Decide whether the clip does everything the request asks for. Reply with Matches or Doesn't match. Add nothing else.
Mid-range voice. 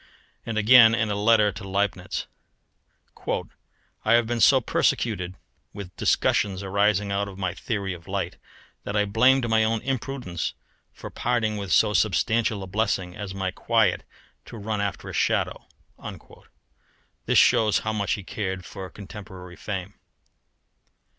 Doesn't match